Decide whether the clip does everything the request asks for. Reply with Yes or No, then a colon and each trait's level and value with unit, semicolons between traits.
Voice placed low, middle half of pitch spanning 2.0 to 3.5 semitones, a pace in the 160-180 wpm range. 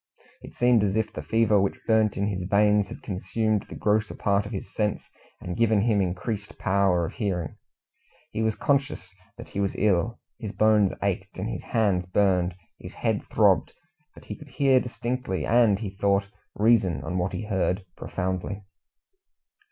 Yes: low, 100 Hz; average, 2.7 semitones; average, 170 wpm